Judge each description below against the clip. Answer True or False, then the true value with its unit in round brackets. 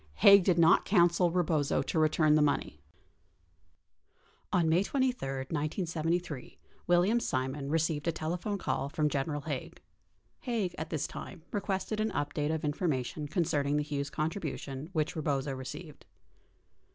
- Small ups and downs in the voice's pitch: False (3.3 semitones)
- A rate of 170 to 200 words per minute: False (140 wpm)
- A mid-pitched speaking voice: True (155 Hz)